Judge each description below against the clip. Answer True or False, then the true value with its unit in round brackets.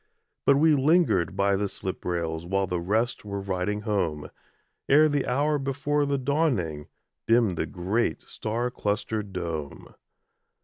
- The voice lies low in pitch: True (105 Hz)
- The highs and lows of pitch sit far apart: True (7.1 semitones)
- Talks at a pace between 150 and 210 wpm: False (140 wpm)